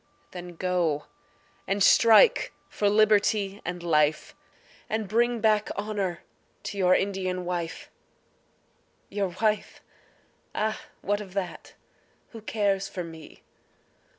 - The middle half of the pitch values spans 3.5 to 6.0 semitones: No, average, 3.0 semitones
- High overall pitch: Yes, high, 195 Hz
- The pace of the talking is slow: Yes, slow, 110 wpm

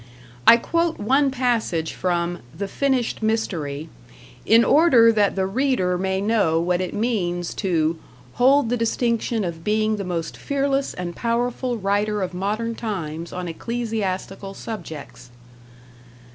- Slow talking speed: Yes, slow, 130 wpm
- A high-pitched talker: Yes, high, 210 Hz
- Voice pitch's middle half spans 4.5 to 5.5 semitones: Yes, average, 4.8 semitones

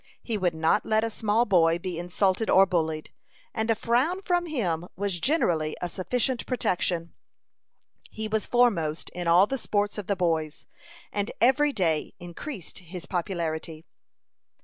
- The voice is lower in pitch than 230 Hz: Yes, high, 190 Hz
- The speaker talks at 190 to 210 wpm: No, average, 150 wpm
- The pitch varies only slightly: No, average, 5.1 semitones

